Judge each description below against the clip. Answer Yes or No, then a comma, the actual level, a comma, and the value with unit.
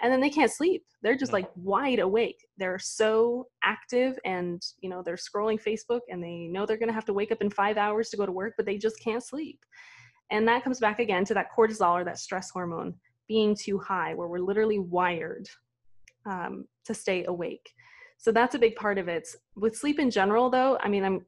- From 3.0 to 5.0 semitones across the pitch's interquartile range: Yes, average, 4.5 semitones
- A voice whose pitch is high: Yes, high, 215 Hz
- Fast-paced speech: Yes, fast, 220 wpm